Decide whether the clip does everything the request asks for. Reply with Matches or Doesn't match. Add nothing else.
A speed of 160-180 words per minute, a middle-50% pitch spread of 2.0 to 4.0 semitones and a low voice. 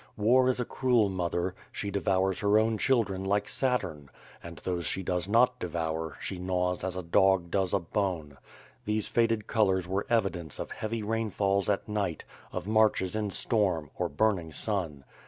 Doesn't match